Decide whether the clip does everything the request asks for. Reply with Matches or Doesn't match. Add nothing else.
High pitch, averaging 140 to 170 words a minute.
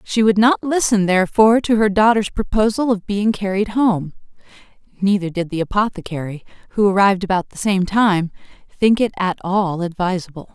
Matches